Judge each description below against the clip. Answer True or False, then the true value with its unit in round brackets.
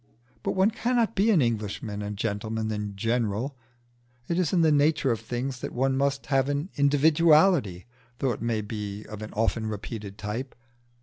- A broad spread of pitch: True (5.7 semitones)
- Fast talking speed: False (175 wpm)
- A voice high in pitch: False (120 Hz)